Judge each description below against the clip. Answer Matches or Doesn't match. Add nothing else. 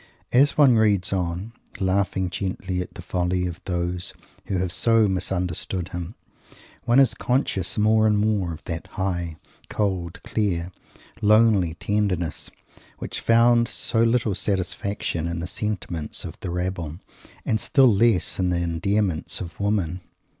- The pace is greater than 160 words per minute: Doesn't match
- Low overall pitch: Matches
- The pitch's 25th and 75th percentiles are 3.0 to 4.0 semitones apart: Matches